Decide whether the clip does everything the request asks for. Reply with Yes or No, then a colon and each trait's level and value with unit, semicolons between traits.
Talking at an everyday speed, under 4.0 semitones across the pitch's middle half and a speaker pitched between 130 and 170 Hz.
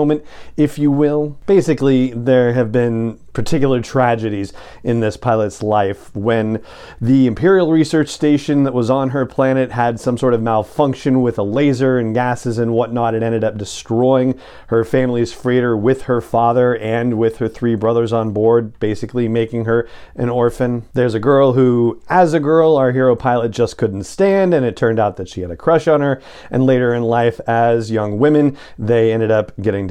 No: average, 185 wpm; average, 2.8 semitones; low, 120 Hz